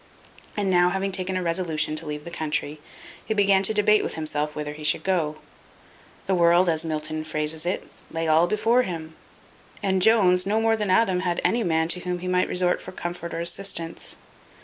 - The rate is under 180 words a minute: No, average, 195 wpm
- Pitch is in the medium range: Yes, medium, 175 Hz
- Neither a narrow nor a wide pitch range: Yes, average, 3.2 semitones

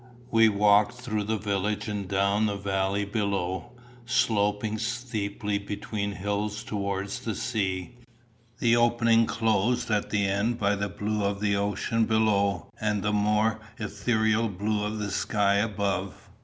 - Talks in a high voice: No, low, 105 Hz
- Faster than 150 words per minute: No, average, 140 wpm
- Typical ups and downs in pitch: No, narrow, 1.6 semitones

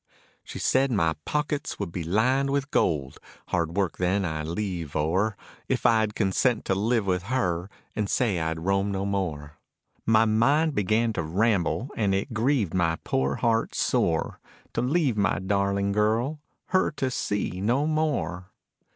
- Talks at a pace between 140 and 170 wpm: Yes, average, 160 wpm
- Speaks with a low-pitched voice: Yes, low, 100 Hz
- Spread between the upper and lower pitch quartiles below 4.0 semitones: No, average, 5.0 semitones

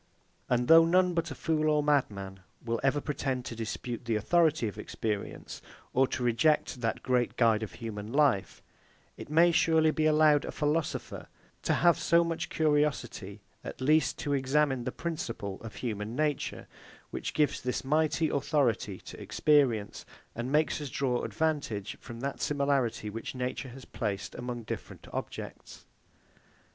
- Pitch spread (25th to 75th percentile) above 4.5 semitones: Yes, average, 4.9 semitones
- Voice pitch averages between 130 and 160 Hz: Yes, low, 135 Hz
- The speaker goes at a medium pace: Yes, average, 155 wpm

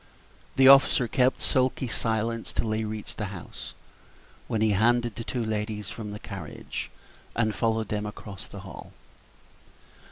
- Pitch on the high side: No, low, 110 Hz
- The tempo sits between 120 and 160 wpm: Yes, average, 150 wpm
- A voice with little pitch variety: Yes, narrow, 2.0 semitones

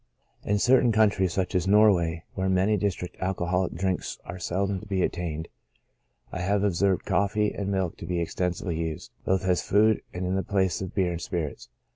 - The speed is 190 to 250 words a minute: Yes, average, 195 wpm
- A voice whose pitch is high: No, very low, 95 Hz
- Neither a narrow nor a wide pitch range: No, narrow, 2.2 semitones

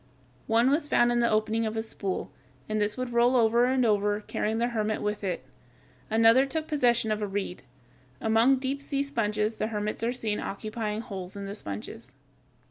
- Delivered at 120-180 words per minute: No, average, 190 wpm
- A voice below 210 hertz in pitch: No, high, 220 Hz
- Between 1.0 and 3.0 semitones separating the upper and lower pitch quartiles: Yes, narrow, 2.5 semitones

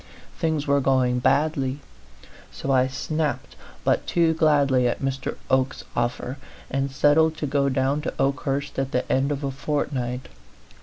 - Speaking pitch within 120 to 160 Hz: Yes, low, 135 Hz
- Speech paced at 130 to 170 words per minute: Yes, average, 150 wpm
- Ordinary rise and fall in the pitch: No, narrow, 2.0 semitones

